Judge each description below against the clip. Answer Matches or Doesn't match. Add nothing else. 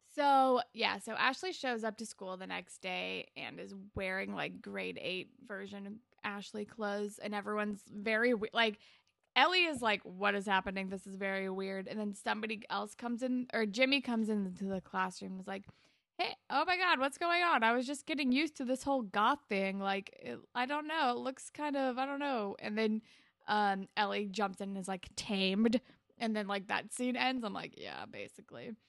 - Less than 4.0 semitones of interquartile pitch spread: Doesn't match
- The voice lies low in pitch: Doesn't match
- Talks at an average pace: Doesn't match